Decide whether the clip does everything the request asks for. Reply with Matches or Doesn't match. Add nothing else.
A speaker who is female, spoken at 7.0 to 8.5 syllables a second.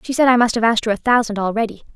Matches